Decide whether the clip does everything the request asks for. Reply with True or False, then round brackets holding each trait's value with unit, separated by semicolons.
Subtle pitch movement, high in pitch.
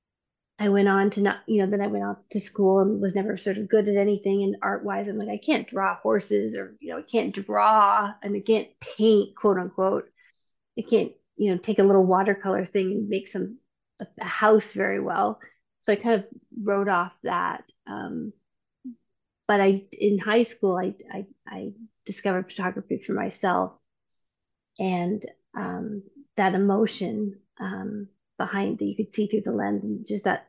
True (1.9 semitones; 205 Hz)